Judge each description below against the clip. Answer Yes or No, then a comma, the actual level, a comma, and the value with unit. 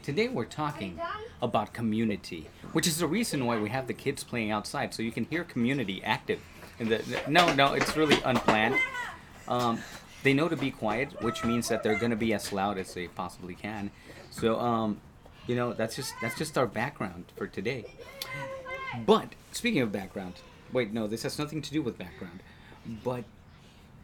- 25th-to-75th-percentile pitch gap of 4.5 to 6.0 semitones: Yes, average, 4.9 semitones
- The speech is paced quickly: No, average, 180 wpm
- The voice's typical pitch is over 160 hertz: No, low, 115 Hz